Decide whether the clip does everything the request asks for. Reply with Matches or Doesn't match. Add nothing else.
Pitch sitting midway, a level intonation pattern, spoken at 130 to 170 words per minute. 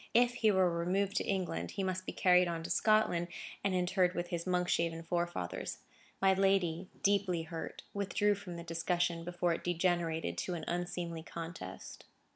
Matches